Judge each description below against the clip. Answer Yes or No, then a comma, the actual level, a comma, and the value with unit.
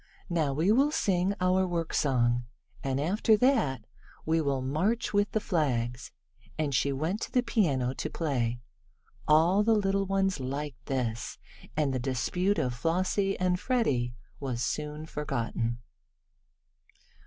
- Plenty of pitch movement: Yes, wide, 6.8 semitones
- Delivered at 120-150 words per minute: Yes, slow, 135 wpm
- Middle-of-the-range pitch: Yes, medium, 155 Hz